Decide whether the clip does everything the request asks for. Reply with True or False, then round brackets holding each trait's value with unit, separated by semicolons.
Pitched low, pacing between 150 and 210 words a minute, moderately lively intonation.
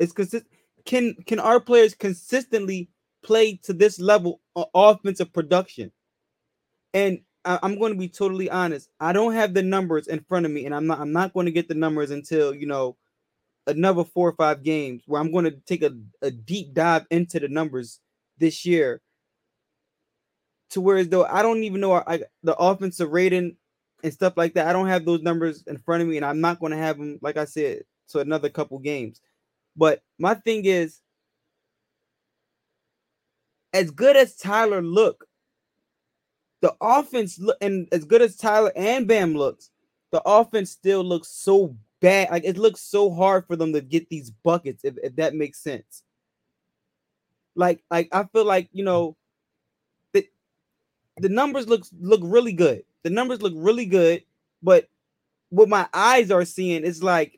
False (180 Hz; 180 wpm; 4.1 semitones)